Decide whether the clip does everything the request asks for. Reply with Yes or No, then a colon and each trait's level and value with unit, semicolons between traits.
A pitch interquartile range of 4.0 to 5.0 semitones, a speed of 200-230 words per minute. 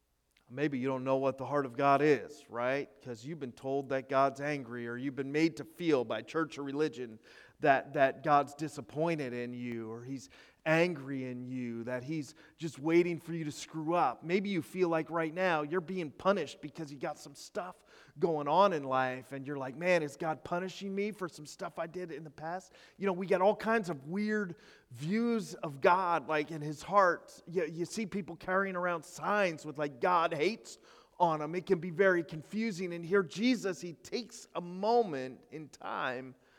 Yes: average, 4.7 semitones; fast, 205 wpm